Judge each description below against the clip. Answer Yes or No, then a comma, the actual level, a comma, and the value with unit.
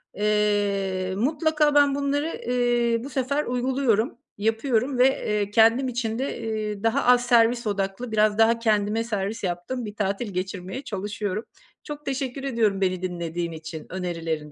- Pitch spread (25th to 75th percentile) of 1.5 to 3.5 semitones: No, average, 4.2 semitones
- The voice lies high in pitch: Yes, high, 220 Hz